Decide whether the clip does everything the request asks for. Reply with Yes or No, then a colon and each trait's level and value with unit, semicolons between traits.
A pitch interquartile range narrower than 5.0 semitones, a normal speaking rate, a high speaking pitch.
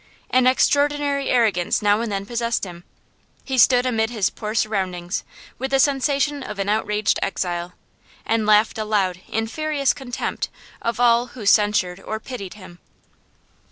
Yes: average, 4.3 semitones; average, 150 wpm; high, 220 Hz